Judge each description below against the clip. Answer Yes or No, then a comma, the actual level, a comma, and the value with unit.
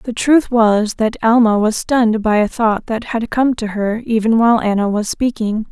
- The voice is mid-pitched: No, high, 225 Hz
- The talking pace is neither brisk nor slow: No, fast, 210 wpm